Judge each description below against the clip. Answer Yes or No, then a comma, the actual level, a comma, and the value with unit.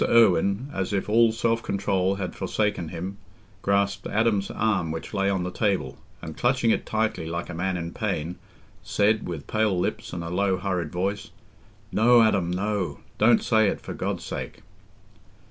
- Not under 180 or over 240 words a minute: No, average, 165 wpm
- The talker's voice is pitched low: Yes, low, 100 Hz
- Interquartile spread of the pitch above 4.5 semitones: No, average, 3.5 semitones